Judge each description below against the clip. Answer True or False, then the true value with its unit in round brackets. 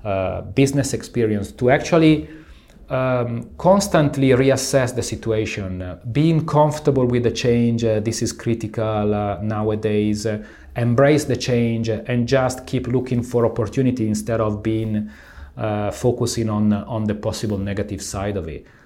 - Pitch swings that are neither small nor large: True (3.4 semitones)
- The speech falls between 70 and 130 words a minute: False (140 wpm)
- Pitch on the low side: True (115 Hz)